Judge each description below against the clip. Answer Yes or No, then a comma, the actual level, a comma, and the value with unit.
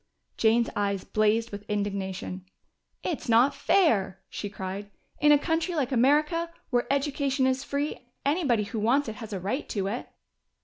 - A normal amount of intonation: No, wide, 5.7 semitones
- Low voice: No, high, 235 Hz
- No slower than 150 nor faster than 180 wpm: Yes, average, 160 wpm